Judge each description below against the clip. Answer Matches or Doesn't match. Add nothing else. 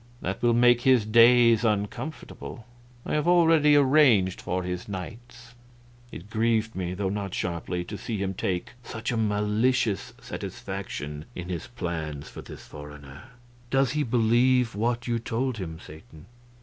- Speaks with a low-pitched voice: Matches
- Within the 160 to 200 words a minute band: Doesn't match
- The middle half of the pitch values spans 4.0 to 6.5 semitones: Matches